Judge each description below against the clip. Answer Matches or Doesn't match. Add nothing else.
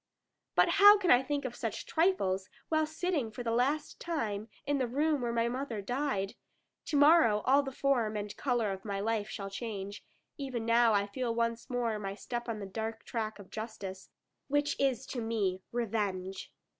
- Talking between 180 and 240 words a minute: Matches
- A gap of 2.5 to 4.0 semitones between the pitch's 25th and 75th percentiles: Doesn't match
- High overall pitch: Matches